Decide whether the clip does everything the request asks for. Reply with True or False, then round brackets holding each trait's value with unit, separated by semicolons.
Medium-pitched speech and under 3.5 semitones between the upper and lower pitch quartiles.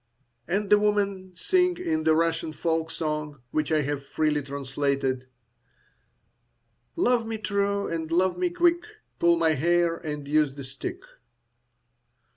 False (165 Hz; 5.1 semitones)